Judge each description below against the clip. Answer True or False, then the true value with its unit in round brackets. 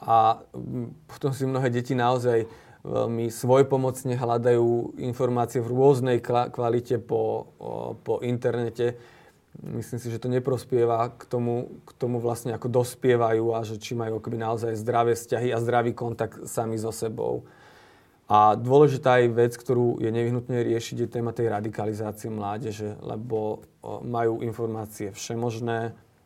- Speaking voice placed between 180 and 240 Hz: False (120 Hz)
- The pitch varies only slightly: True (1.5 semitones)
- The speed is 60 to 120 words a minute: False (135 wpm)